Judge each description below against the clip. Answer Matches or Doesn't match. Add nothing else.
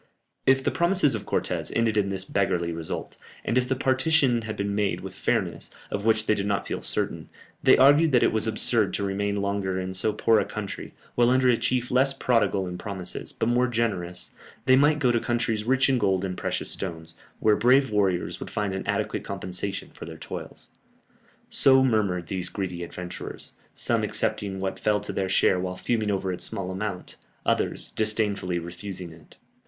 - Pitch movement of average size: Matches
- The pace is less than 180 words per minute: Doesn't match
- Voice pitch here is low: Matches